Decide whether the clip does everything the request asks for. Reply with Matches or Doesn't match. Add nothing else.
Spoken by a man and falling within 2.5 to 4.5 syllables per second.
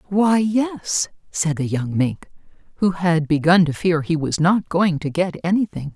Doesn't match